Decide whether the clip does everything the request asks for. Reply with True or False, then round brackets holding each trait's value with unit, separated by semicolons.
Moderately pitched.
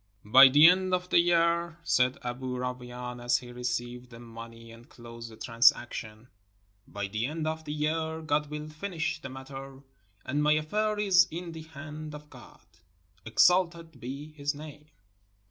True (145 Hz)